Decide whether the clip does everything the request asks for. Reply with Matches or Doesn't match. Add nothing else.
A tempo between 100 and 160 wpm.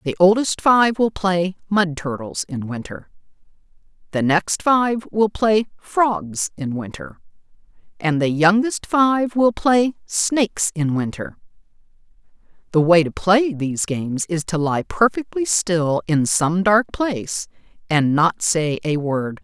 Matches